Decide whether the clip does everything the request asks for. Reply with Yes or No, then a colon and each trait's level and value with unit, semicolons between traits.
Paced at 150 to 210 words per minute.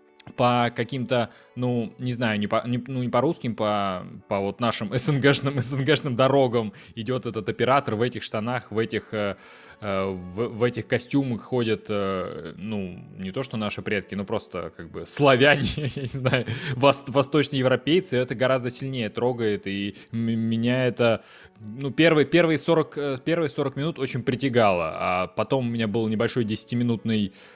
Yes: average, 155 wpm